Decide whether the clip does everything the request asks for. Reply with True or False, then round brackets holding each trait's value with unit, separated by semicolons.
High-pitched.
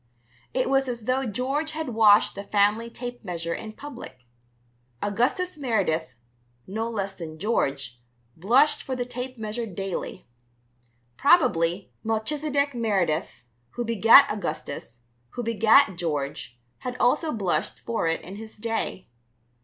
True (220 Hz)